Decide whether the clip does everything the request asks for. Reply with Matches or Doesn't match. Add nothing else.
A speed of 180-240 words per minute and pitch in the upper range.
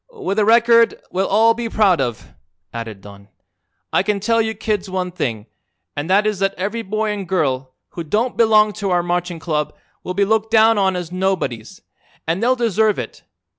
Matches